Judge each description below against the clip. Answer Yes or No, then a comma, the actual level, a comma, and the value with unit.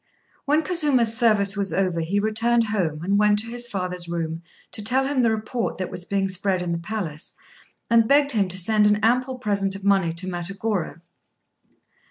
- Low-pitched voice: No, high, 205 Hz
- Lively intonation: No, average, 4.0 semitones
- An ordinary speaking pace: Yes, average, 190 wpm